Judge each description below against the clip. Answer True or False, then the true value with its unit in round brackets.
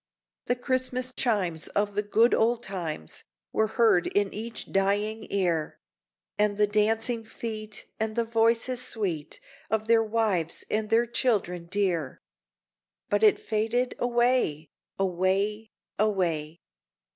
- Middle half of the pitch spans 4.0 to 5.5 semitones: False (3.0 semitones)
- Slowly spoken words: True (120 wpm)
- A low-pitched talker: False (215 Hz)